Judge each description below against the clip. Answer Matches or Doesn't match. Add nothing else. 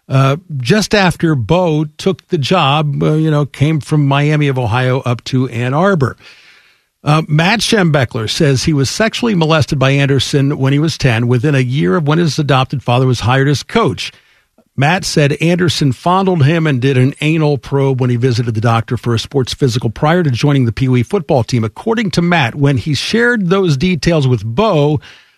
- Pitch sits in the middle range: Matches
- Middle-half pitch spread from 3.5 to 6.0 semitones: Matches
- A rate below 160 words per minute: Doesn't match